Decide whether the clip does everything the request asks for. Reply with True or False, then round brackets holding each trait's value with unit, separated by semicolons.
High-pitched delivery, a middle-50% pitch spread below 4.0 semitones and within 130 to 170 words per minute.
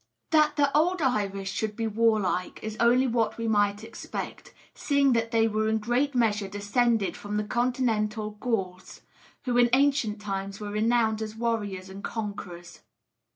True (220 Hz; 2.8 semitones; 155 wpm)